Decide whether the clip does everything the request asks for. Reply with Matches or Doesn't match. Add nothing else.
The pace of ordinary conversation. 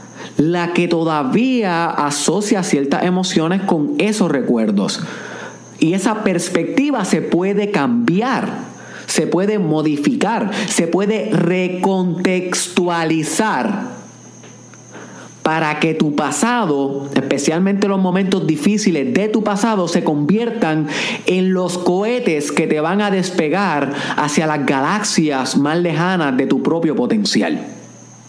Doesn't match